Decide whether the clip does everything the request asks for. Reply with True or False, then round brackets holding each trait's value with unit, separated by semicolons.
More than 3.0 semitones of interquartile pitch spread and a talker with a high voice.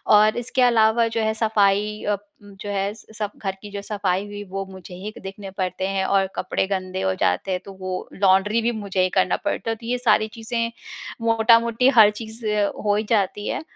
False (2.4 semitones; 205 Hz)